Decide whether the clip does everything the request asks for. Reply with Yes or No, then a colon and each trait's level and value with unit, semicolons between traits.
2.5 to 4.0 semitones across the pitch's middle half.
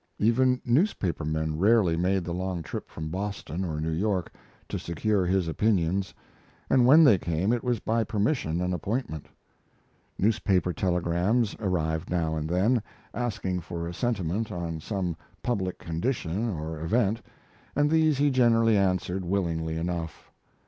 No: average, 5.2 semitones